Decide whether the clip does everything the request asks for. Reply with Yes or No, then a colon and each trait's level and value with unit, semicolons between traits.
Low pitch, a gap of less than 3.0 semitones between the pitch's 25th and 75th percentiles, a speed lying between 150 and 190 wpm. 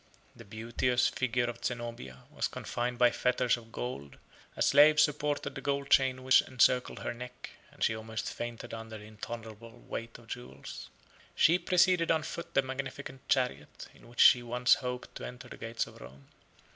Yes: low, 125 Hz; narrow, 2.5 semitones; average, 175 wpm